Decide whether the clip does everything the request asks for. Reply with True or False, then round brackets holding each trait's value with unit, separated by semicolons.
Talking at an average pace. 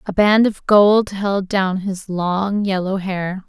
True (170 wpm)